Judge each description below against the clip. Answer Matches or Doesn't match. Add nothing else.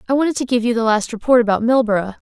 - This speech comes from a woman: Matches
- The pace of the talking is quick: Matches